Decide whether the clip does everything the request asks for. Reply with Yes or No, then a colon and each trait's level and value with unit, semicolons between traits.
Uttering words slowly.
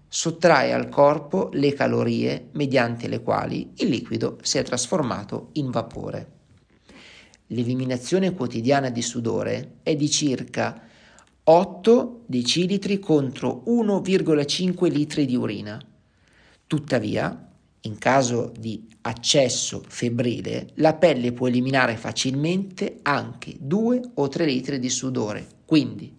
Yes: slow, 110 wpm